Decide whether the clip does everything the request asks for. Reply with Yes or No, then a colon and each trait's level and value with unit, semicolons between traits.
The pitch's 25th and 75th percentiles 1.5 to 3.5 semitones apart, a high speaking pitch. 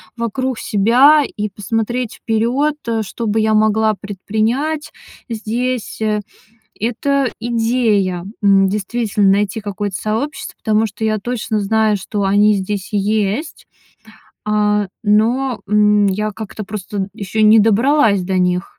Yes: narrow, 2.4 semitones; high, 215 Hz